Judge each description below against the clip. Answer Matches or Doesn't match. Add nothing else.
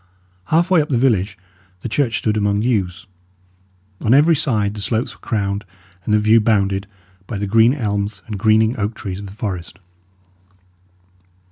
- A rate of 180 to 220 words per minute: Doesn't match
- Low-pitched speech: Matches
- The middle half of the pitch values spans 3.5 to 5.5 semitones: Doesn't match